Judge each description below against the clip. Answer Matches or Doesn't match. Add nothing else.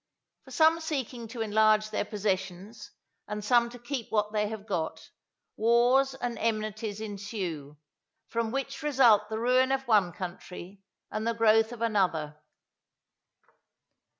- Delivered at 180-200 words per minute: Doesn't match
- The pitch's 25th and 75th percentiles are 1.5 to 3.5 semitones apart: Matches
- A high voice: Matches